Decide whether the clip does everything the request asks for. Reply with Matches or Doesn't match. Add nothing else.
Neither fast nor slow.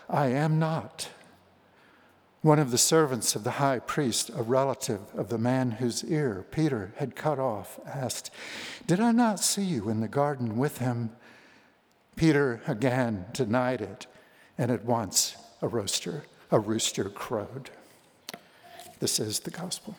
Matches